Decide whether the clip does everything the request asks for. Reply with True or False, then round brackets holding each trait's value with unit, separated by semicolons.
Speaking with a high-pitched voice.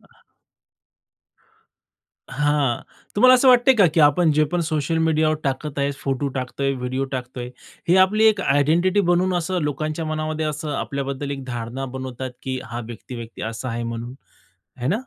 False (145 Hz)